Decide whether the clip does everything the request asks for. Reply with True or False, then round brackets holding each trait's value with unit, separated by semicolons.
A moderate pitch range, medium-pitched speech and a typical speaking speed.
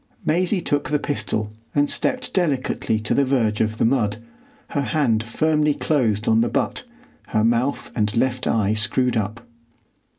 False (4.9 semitones; 120 Hz; 160 wpm)